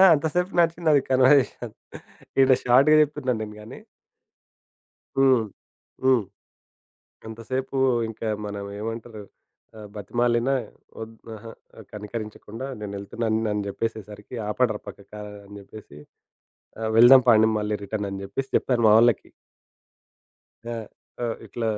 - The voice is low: Yes, low, 115 Hz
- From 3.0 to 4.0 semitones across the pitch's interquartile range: Yes, average, 3.5 semitones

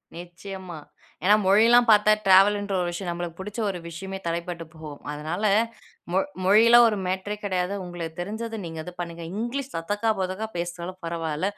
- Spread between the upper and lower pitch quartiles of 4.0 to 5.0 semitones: No, average, 3.3 semitones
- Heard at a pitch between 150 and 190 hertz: Yes, medium, 185 Hz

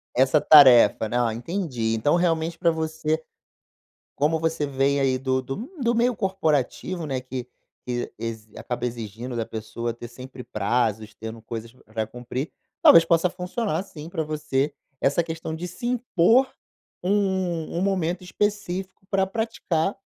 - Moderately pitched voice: Yes, medium, 155 Hz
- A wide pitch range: Yes, wide, 6.6 semitones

